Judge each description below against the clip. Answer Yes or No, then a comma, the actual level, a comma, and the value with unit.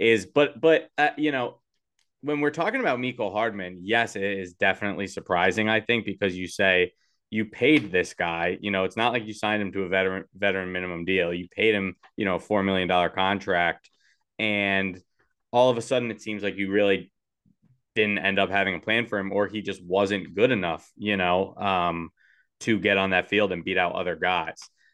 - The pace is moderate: No, fast, 210 wpm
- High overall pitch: No, low, 100 Hz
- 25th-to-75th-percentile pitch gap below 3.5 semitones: Yes, average, 2.9 semitones